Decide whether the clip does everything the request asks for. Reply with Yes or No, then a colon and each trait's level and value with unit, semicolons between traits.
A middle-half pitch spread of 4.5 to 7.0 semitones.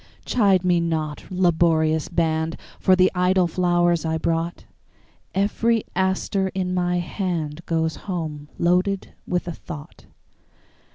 No: narrow, 2.4 semitones